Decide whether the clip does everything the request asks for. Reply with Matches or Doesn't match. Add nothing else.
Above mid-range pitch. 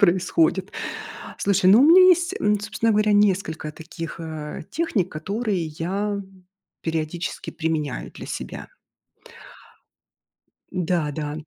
Doesn't match